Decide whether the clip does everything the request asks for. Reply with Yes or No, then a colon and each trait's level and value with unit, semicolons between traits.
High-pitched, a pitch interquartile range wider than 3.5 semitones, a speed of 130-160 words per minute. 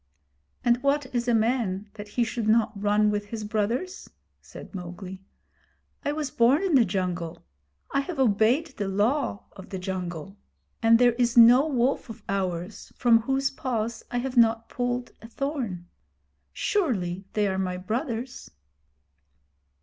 Yes: high, 225 Hz; average, 4.2 semitones; average, 150 wpm